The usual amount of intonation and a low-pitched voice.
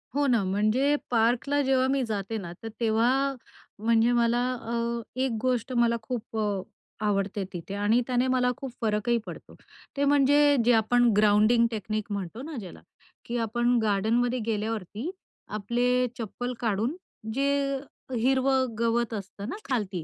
No: average, 3.2 semitones; high, 235 Hz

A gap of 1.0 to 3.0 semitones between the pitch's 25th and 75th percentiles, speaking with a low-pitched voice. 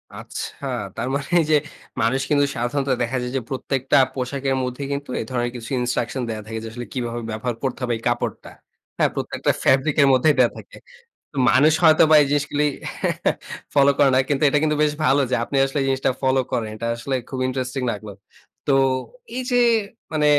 Yes: average, 2.7 semitones; low, 130 Hz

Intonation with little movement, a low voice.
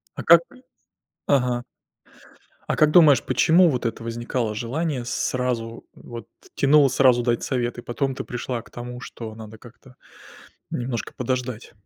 Yes: narrow, 2.1 semitones; low, 125 Hz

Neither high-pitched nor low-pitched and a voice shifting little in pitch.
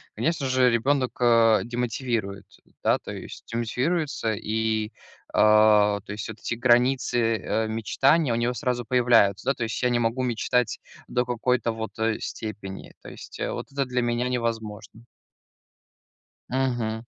No: low, 120 Hz; narrow, 2.3 semitones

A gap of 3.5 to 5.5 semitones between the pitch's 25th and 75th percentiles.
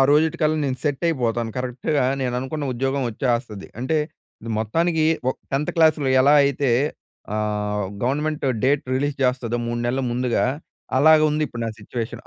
Yes: average, 3.9 semitones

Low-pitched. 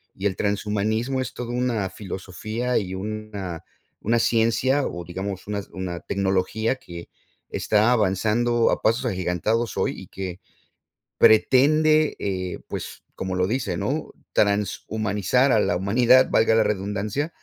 Yes: low, 105 Hz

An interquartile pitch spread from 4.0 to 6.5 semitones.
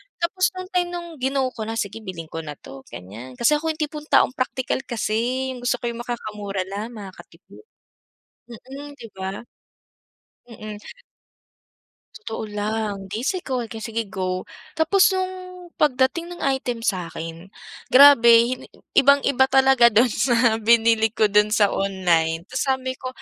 Yes: average, 4.6 semitones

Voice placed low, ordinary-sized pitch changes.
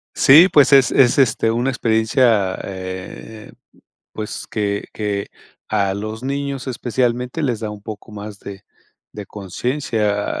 Yes: low, 110 Hz; average, 3.8 semitones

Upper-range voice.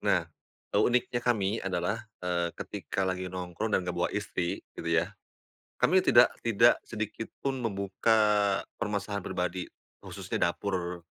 No: low, 100 Hz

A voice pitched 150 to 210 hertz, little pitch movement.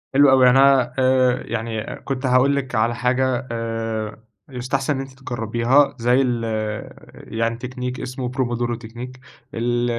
No: low, 125 Hz; narrow, 2.1 semitones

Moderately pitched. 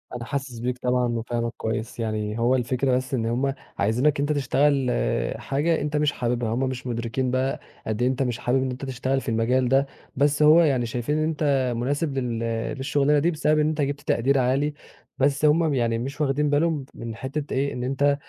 No: low, 130 Hz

